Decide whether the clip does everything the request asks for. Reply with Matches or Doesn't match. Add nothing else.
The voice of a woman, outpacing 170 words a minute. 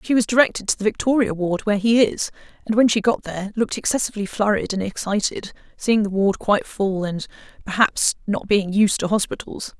Matches